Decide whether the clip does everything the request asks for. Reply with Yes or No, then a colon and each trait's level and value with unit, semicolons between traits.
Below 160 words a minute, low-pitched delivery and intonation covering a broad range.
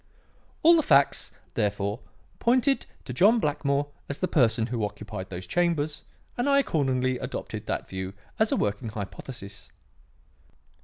Yes: average, 140 wpm; low, 130 Hz; wide, 9.0 semitones